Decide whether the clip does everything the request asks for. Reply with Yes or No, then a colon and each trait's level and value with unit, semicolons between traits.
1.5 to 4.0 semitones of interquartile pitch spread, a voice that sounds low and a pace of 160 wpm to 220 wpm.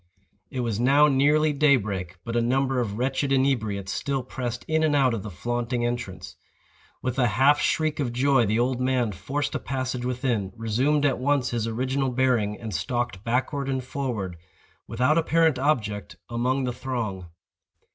Yes: average, 3.0 semitones; low, 125 Hz; average, 170 wpm